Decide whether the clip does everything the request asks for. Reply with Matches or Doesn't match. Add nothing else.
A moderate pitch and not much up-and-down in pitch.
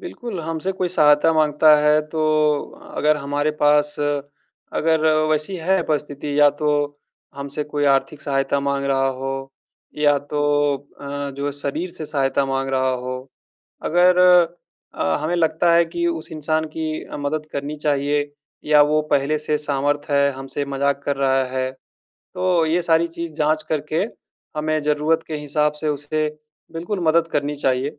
Matches